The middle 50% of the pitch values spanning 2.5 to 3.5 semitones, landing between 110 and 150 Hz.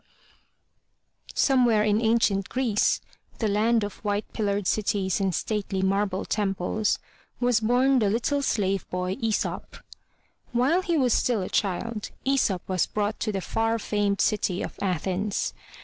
No: average, 2.9 semitones; high, 210 Hz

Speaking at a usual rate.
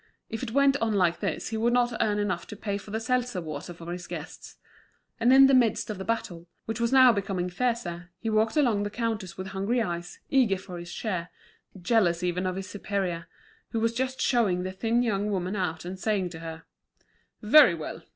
No: fast, 210 wpm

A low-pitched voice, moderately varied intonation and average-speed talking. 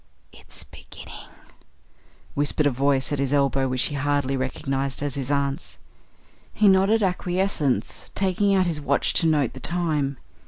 No: medium, 145 Hz; average, 4.4 semitones; average, 150 wpm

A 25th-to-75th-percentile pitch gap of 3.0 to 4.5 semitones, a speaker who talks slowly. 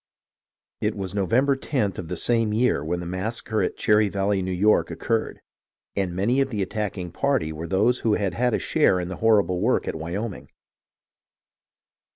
No: average, 3.8 semitones; average, 180 wpm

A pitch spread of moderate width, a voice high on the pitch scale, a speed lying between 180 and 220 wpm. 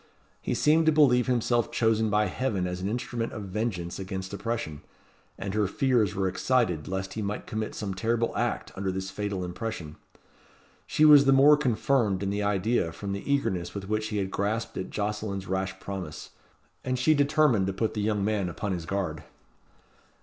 No: average, 3.8 semitones; low, 105 Hz; average, 185 wpm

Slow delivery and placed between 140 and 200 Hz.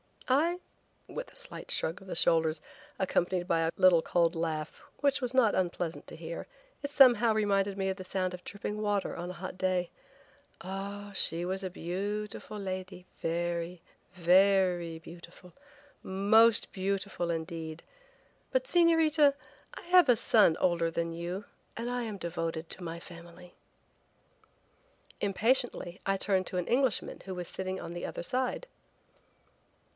No: average, 150 wpm; medium, 185 Hz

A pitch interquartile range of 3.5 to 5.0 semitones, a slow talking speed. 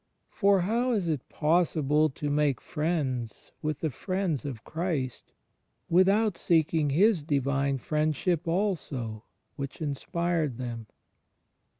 Yes: average, 4.2 semitones; slow, 110 wpm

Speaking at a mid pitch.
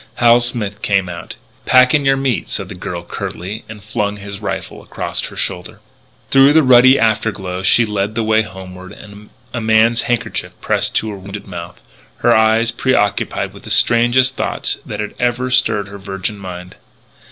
No: low, 110 Hz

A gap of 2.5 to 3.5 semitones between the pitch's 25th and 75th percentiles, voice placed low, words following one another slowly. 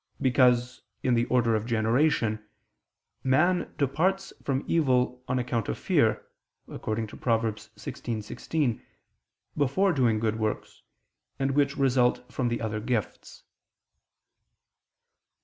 Yes: average, 3.2 semitones; low, 125 Hz; slow, 105 wpm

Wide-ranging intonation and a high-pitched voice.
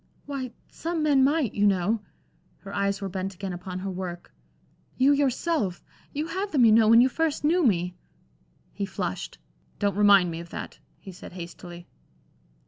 Yes: wide, 7.1 semitones; high, 205 Hz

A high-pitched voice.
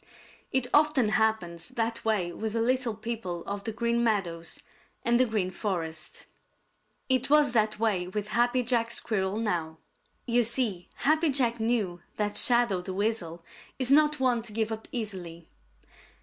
Yes: high, 220 Hz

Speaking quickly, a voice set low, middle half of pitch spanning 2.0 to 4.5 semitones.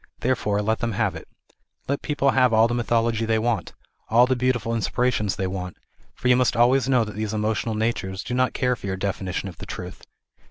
Yes: fast, 215 wpm; low, 115 Hz; average, 2.9 semitones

